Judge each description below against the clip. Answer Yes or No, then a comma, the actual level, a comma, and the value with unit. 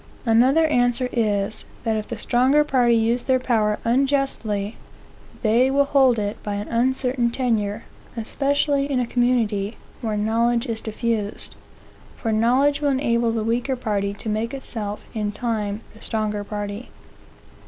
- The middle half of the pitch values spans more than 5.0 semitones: No, average, 3.1 semitones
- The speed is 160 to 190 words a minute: No, average, 145 wpm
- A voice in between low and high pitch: No, high, 235 Hz